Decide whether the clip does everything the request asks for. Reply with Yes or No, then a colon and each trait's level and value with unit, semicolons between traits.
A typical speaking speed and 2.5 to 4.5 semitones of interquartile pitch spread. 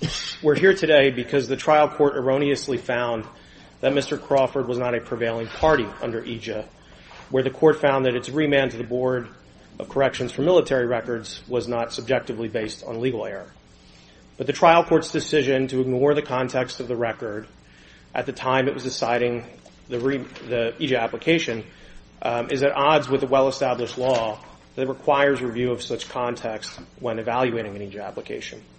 Yes: average, 170 wpm; average, 3.0 semitones